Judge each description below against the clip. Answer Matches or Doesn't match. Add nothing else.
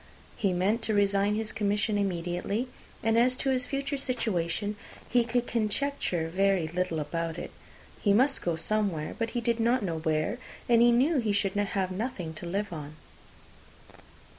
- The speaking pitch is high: Matches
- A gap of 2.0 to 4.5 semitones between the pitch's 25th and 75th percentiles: Doesn't match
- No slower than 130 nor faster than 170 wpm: Matches